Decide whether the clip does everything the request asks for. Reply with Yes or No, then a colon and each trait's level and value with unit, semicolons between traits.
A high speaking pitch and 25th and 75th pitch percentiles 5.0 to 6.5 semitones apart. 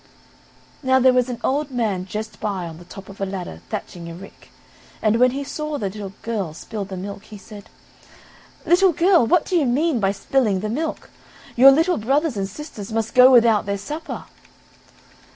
Yes: high, 225 Hz; wide, 5.6 semitones